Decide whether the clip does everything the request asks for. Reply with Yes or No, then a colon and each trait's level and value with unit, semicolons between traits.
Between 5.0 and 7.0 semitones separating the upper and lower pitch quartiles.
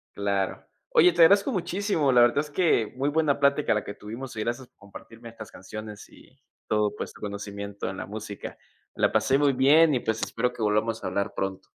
Yes: wide, 5.5 semitones